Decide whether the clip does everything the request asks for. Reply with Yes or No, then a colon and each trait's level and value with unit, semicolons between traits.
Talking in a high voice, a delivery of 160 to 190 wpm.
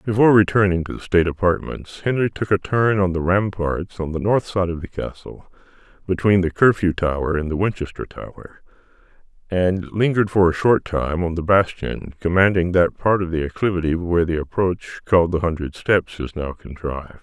No: very low, 90 Hz; average, 185 wpm